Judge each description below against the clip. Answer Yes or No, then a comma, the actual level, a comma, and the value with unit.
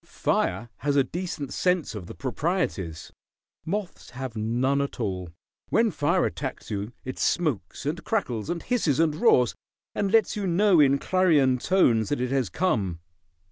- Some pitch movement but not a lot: No, wide, 7.4 semitones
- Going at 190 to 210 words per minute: No, average, 160 wpm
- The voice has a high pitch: No, medium, 140 Hz